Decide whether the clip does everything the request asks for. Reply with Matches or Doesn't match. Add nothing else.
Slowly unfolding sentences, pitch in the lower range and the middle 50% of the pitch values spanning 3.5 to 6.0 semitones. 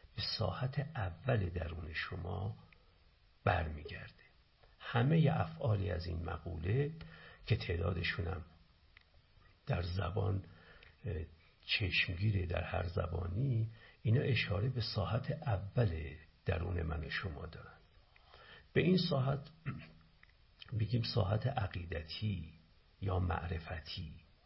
Matches